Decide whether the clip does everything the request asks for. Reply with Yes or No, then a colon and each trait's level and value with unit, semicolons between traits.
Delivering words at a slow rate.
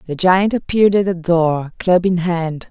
No: average, 200 wpm